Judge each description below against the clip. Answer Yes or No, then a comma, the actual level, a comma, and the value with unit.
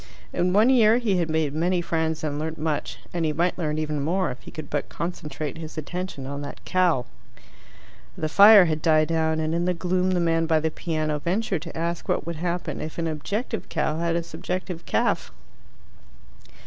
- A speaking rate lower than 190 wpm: No, average, 200 wpm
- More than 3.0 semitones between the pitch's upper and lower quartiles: No, narrow, 2.5 semitones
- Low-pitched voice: No, medium, 165 Hz